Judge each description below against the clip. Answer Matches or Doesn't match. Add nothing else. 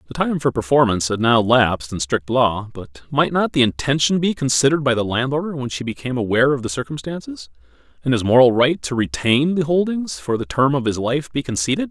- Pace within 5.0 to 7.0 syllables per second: Matches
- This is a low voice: Matches